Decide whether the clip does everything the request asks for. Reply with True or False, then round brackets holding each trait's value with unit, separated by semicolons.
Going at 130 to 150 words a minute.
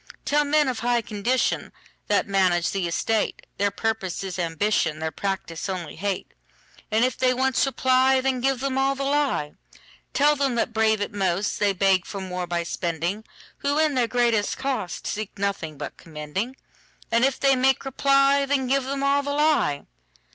True (145 wpm)